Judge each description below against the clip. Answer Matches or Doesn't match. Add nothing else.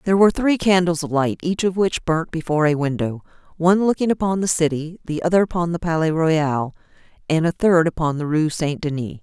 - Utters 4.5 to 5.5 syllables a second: Doesn't match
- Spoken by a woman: Matches